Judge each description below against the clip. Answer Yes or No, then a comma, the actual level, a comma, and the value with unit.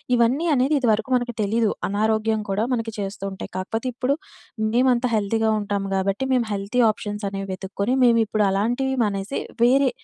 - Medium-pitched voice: No, high, 220 Hz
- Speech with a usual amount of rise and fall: Yes, average, 3.4 semitones